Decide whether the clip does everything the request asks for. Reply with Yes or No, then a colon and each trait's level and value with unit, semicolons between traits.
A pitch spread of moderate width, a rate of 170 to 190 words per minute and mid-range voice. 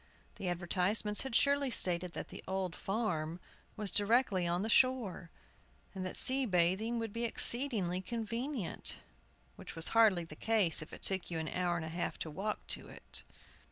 No: average, 4.6 semitones; average, 175 wpm; high, 195 Hz